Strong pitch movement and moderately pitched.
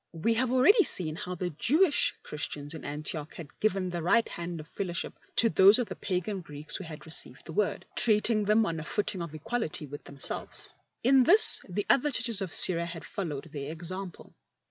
Yes: wide, 5.8 semitones; medium, 180 Hz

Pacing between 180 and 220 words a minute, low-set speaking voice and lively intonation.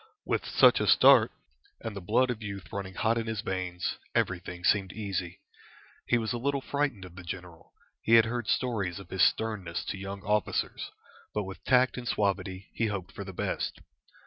No: average, 190 wpm; low, 100 Hz; average, 3.3 semitones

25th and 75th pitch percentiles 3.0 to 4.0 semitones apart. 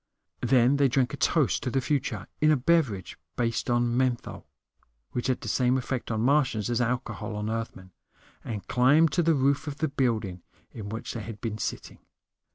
Yes: average, 3.6 semitones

